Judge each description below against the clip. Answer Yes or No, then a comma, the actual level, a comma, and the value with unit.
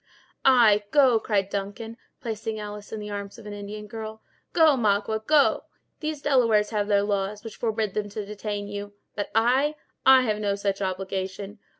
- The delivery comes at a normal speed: Yes, average, 170 wpm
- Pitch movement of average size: No, narrow, 2.0 semitones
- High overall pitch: Yes, high, 210 Hz